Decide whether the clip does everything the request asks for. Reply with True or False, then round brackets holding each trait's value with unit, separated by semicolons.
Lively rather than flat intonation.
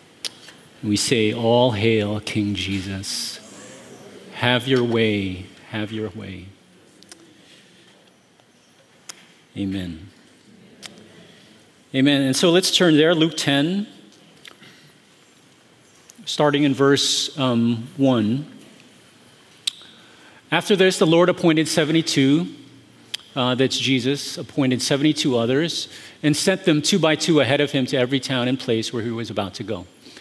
True (5.7 semitones)